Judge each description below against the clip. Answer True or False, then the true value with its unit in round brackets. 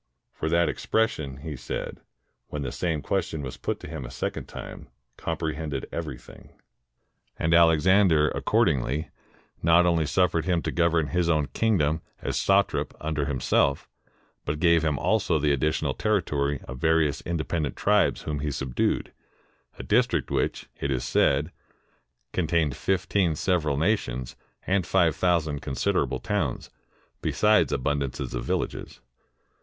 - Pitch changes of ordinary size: True (3.4 semitones)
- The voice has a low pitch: True (80 Hz)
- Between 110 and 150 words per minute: True (140 wpm)